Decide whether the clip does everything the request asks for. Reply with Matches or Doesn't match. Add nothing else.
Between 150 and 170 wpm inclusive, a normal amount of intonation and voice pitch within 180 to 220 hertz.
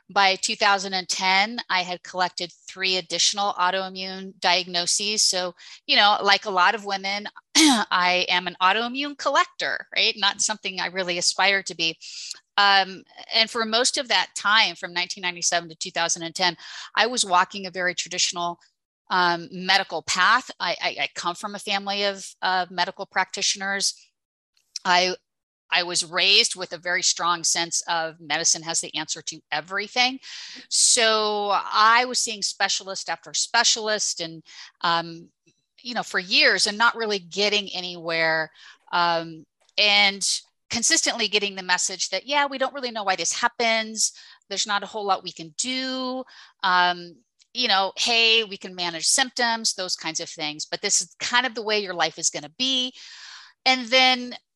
Matches